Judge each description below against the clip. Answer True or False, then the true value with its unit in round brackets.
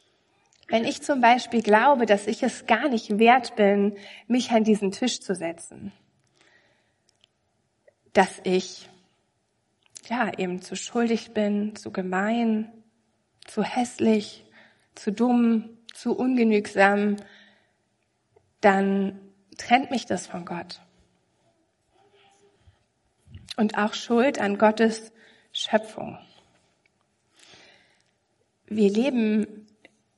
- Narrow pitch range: False (3.0 semitones)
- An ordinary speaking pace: False (95 wpm)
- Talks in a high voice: True (215 Hz)